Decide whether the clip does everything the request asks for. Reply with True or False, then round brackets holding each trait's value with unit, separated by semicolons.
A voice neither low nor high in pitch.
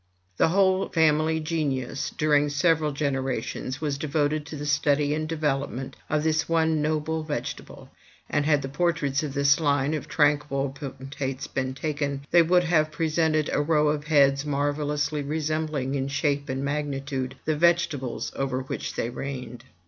True (145 Hz)